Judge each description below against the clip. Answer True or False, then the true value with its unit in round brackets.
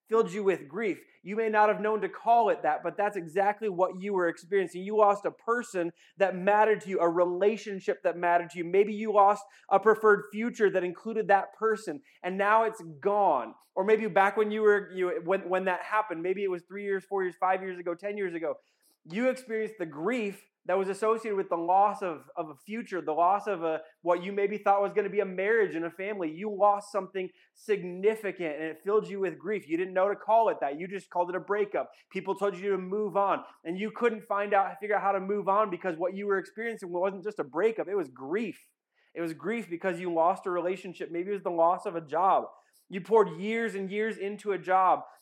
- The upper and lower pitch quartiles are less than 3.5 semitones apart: True (2.7 semitones)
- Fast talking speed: True (240 wpm)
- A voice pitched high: True (195 Hz)